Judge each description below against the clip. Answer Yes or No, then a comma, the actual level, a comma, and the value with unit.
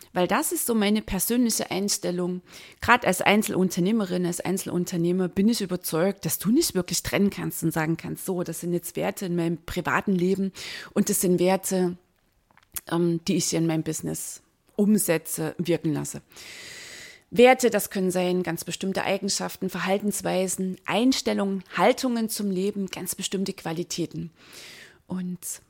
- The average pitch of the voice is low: No, medium, 185 Hz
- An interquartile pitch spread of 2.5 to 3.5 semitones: Yes, average, 2.8 semitones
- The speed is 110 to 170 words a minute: Yes, average, 145 wpm